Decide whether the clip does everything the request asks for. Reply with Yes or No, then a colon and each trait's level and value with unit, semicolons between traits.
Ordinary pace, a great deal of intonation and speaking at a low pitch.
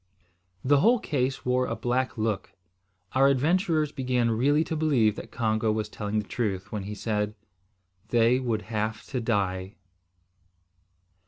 No: average, 145 wpm; average, 3.8 semitones; low, 115 Hz